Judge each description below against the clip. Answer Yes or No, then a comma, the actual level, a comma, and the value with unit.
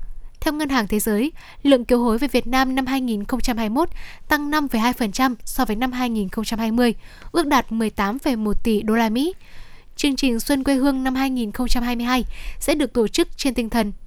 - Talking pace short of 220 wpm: Yes, average, 170 wpm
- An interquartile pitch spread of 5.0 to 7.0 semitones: No, average, 3.2 semitones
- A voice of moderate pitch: No, very high, 250 Hz